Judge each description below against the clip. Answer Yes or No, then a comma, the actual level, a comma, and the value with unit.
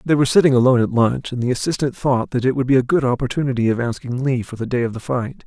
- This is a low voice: Yes, low, 125 Hz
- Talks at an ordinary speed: No, fast, 285 wpm